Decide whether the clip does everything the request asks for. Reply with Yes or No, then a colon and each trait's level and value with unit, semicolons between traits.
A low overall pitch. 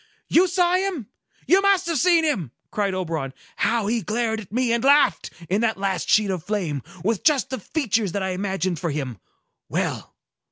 No: high, 215 Hz